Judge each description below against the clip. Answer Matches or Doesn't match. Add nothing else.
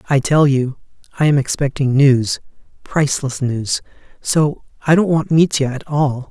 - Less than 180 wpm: Matches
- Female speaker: Doesn't match